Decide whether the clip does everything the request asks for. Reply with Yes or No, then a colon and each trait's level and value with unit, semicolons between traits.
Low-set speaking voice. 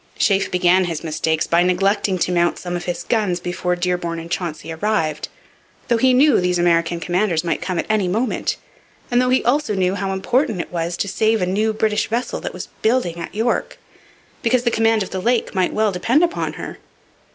No: medium, 185 Hz